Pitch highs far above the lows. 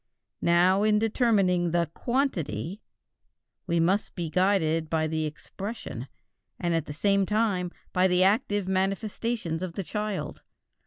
No: average, 3.8 semitones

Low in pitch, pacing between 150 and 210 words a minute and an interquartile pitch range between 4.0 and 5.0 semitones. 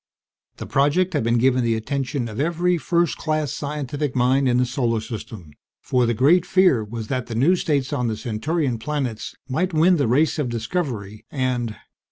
Yes: low, 130 Hz; average, 185 wpm; average, 4.6 semitones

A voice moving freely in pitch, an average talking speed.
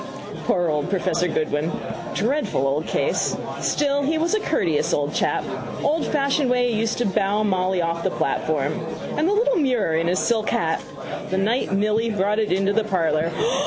Yes: wide, 6.9 semitones; average, 175 wpm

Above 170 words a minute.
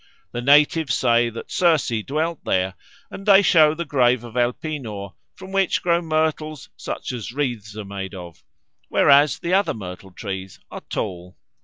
No: average, 160 wpm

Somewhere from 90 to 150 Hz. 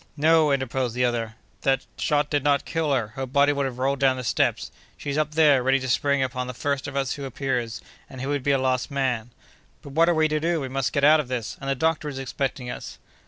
Yes: low, 135 Hz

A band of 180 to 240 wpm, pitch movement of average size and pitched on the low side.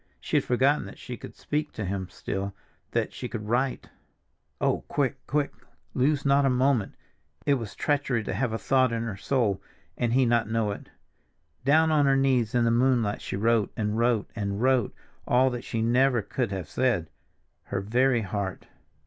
Yes: average, 185 wpm; average, 3.9 semitones; low, 120 Hz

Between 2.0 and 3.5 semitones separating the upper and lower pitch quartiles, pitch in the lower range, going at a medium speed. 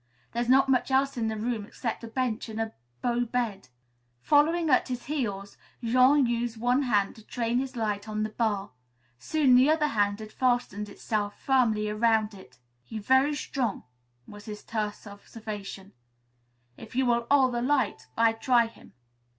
No: average, 3.2 semitones; high, 230 Hz; average, 170 wpm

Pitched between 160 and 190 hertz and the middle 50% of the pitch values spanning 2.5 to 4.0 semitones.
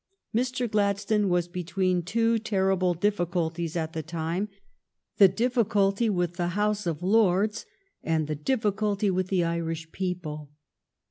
Yes: medium, 185 Hz; average, 3.6 semitones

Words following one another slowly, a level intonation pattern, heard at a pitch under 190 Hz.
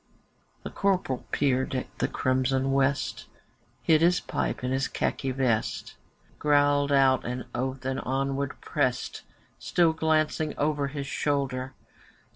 Yes: slow, 125 wpm; narrow, 1.9 semitones; low, 135 Hz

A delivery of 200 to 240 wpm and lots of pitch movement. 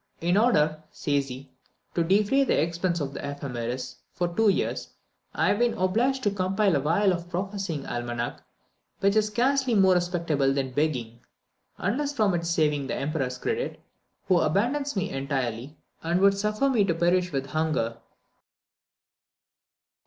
No: average, 150 wpm; wide, 6.4 semitones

